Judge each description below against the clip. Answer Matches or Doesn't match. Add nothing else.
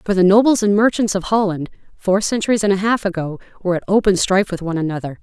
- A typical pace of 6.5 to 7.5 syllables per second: Matches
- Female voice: Matches